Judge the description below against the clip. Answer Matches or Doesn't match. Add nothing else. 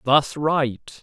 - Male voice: Matches